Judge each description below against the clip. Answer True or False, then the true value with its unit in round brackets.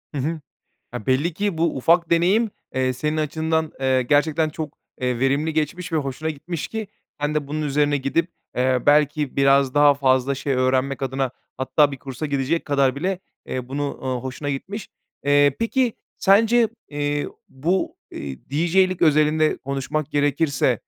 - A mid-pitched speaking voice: True (145 Hz)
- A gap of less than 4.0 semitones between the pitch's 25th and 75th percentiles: True (3.1 semitones)